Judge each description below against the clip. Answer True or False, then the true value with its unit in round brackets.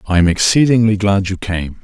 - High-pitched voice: False (100 Hz)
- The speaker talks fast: False (195 wpm)